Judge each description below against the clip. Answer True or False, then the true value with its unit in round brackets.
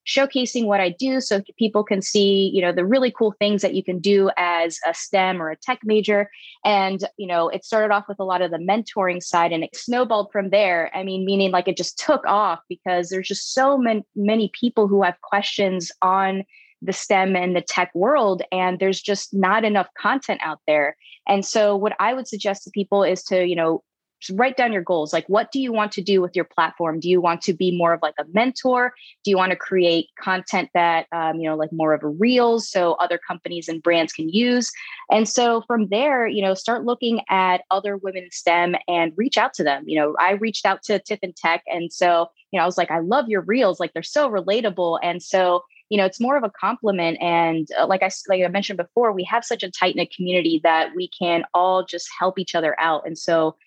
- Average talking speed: False (235 wpm)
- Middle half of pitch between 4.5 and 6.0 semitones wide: False (3.3 semitones)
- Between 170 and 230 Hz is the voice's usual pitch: True (190 Hz)